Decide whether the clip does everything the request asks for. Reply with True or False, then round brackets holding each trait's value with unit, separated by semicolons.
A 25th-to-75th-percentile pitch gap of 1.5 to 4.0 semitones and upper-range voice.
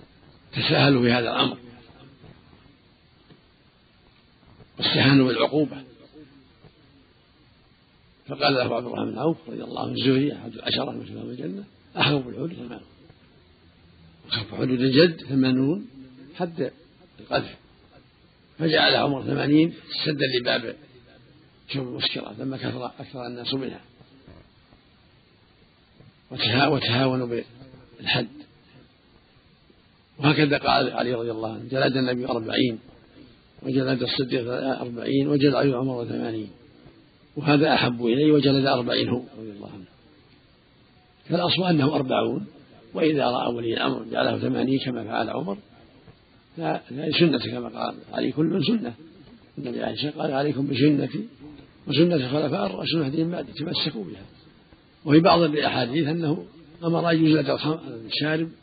False (3.6 semitones; 135 Hz)